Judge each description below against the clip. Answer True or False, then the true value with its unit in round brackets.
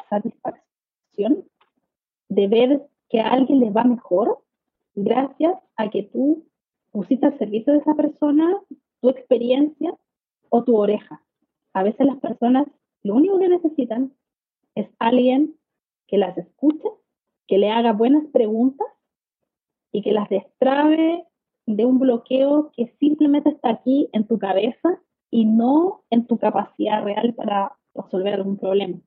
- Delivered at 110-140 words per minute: True (135 wpm)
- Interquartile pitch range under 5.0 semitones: False (5.6 semitones)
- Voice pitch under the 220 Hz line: False (250 Hz)